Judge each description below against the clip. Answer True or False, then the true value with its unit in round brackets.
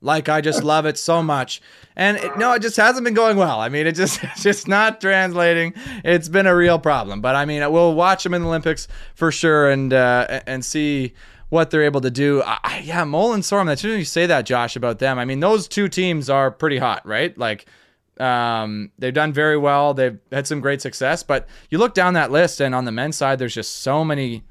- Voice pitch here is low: False (155 Hz)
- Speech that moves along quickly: True (240 wpm)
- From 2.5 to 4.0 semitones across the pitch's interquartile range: False (4.9 semitones)